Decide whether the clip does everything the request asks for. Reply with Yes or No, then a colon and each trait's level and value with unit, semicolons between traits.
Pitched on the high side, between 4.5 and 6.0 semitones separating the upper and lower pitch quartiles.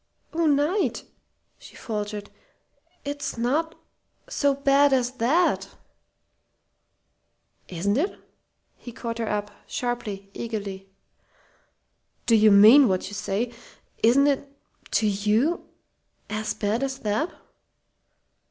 Yes: high, 230 Hz; average, 5.1 semitones